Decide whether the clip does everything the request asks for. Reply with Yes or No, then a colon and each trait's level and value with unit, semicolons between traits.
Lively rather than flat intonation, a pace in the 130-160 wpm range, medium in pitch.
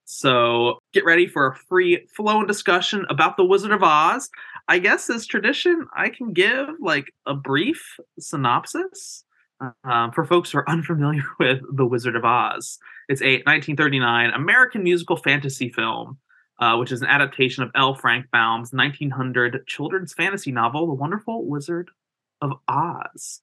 Yes: wide, 6.5 semitones; average, 155 wpm; medium, 150 Hz